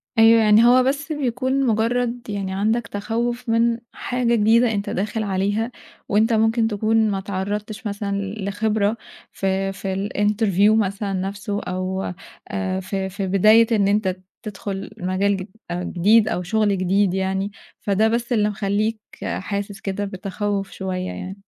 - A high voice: Yes, high, 205 Hz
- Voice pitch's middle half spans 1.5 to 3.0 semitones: Yes, narrow, 2.4 semitones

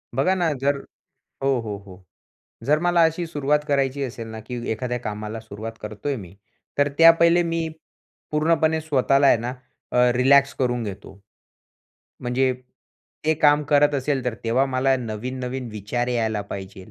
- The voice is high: No, low, 130 Hz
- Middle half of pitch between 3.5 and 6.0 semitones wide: Yes, average, 4.5 semitones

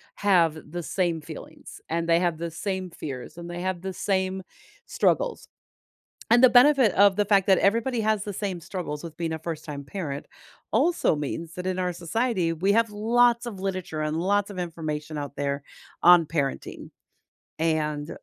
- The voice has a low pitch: No, medium, 180 Hz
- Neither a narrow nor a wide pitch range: Yes, average, 4.1 semitones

